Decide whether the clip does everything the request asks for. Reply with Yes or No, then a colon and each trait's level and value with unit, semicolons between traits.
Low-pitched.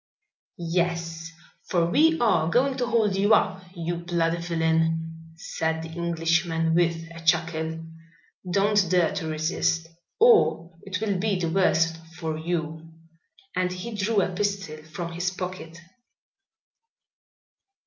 No: medium, 170 Hz